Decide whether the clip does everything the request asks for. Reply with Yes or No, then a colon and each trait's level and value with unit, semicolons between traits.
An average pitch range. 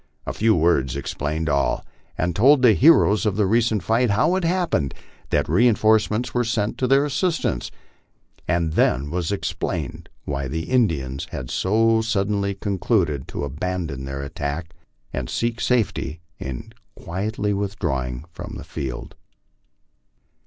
No: wide, 7.2 semitones